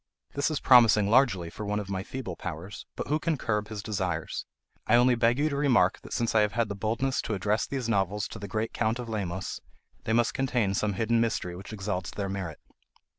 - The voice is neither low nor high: No, low, 110 Hz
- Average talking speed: No, fast, 225 wpm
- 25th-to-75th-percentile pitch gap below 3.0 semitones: No, average, 3.3 semitones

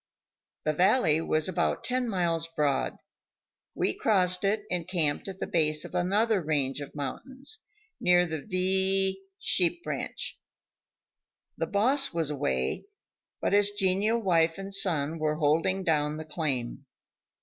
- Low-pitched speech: No, medium, 180 Hz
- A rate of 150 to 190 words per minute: No, average, 140 wpm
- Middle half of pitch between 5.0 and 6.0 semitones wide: No, average, 4.1 semitones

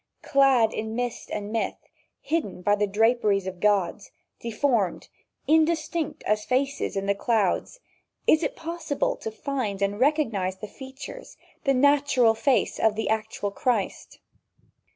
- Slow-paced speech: Yes, slow, 130 wpm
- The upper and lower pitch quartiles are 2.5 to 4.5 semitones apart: No, average, 5.3 semitones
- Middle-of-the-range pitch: No, high, 225 Hz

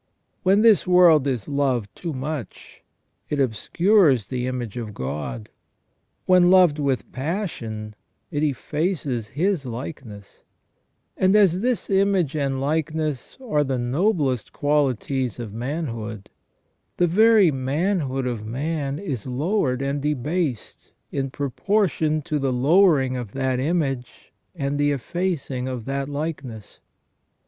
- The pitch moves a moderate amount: Yes, average, 4.9 semitones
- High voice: No, medium, 140 Hz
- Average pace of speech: No, slow, 120 wpm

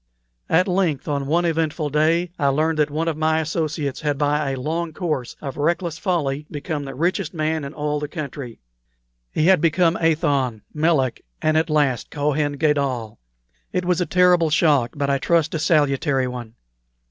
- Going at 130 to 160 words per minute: No, average, 175 wpm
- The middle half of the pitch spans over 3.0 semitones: No, narrow, 2.6 semitones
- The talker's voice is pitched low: No, medium, 150 Hz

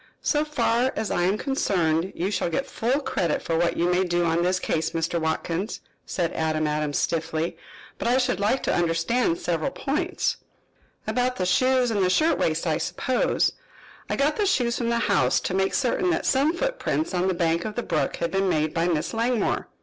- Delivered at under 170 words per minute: No, average, 200 wpm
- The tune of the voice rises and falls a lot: Yes, wide, 7.1 semitones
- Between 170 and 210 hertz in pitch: Yes, medium, 185 Hz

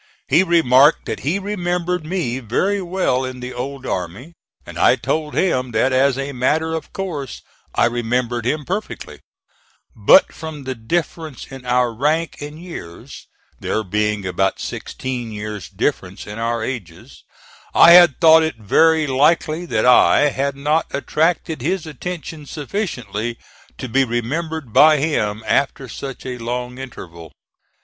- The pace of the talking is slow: No, average, 145 wpm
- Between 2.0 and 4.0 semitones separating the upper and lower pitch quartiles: No, average, 5.2 semitones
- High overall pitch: No, low, 135 Hz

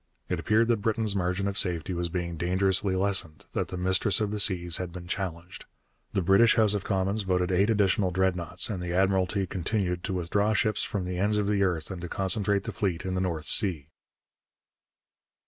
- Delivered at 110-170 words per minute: No, average, 200 wpm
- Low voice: Yes, very low, 95 Hz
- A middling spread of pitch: No, narrow, 2.3 semitones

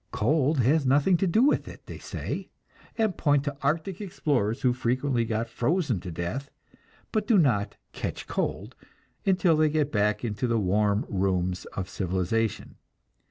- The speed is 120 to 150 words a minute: No, average, 160 wpm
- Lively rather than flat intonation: Yes, wide, 7.0 semitones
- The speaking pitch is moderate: No, low, 125 Hz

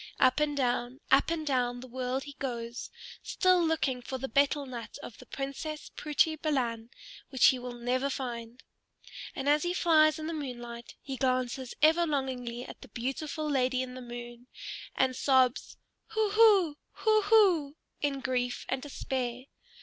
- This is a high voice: Yes, very high, 265 Hz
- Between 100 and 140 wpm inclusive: No, average, 165 wpm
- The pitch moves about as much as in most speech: Yes, average, 3.6 semitones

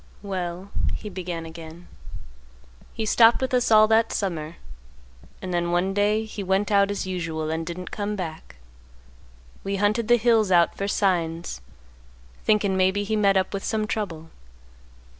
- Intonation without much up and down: No, average, 3.5 semitones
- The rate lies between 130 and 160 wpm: Yes, average, 155 wpm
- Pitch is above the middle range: Yes, high, 195 Hz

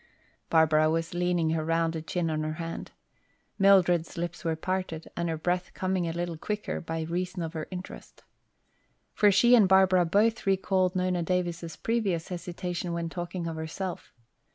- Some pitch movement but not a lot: No, narrow, 2.2 semitones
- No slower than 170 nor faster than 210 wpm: No, average, 160 wpm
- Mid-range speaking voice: Yes, medium, 175 Hz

